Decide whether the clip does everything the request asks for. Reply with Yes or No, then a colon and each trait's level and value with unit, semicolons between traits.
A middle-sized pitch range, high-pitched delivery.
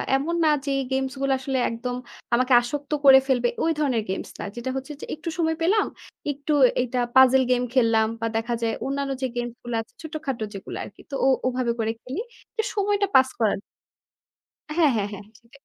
Yes: average, 3.2 semitones; very high, 260 Hz